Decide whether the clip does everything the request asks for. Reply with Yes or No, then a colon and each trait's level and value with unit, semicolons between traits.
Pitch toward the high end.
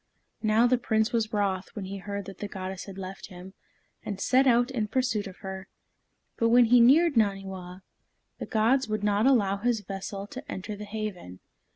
Yes: high, 210 Hz